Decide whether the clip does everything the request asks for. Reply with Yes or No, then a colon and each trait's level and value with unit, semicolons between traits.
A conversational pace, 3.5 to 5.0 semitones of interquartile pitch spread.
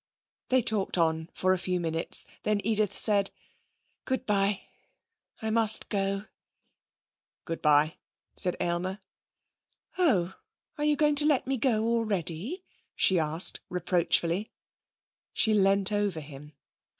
No: slow, 125 wpm; average, 4.3 semitones